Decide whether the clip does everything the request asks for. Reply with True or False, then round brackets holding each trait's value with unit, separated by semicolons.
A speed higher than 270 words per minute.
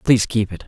False (265 wpm)